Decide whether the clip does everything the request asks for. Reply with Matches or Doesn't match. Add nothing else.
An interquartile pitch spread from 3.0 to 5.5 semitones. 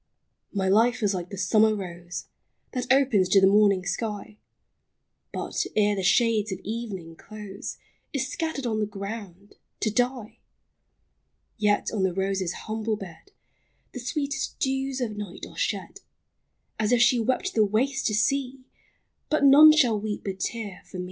Matches